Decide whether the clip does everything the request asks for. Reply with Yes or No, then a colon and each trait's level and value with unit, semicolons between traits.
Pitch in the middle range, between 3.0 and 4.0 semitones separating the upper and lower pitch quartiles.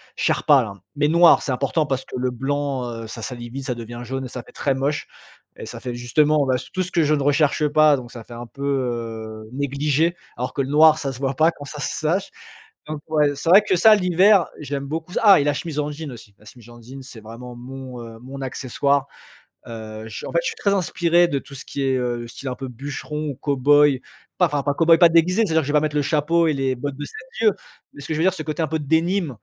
Yes: medium, 145 Hz; average, 3.6 semitones